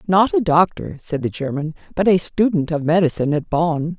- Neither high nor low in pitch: Yes, medium, 170 Hz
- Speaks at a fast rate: No, average, 195 wpm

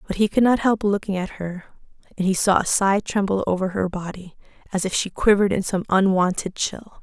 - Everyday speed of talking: No, fast, 215 wpm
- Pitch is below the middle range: No, high, 195 Hz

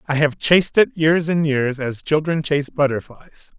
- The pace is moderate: Yes, average, 185 wpm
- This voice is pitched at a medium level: Yes, medium, 150 Hz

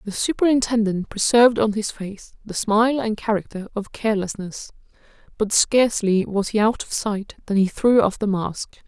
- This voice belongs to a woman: Yes, female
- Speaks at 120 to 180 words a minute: Yes, average, 170 wpm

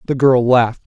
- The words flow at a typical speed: Yes, average, 180 wpm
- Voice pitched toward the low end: Yes, low, 125 Hz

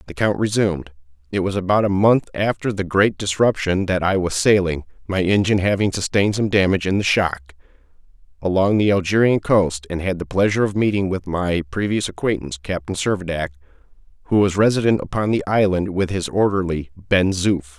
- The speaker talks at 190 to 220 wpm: No, average, 170 wpm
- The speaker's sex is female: No, male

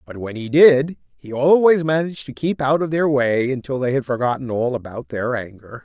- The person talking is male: Yes, male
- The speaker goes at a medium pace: No, fast, 215 wpm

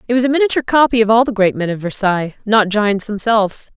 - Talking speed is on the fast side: Yes, fast, 240 wpm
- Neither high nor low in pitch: No, high, 220 Hz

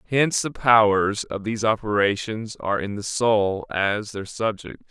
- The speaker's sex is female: No, male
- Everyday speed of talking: Yes, average, 160 wpm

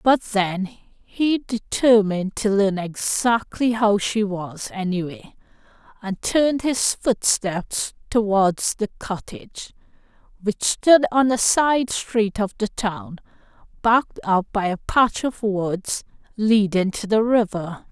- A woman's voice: Yes, female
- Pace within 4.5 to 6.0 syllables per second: No, 3.6 syllables/s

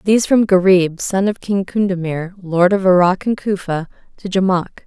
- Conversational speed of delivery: Yes, average, 175 wpm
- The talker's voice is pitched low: No, high, 190 Hz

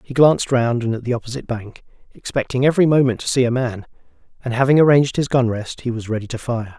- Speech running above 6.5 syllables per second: Yes, 6.7 syllables/s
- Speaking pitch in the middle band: No, low, 125 Hz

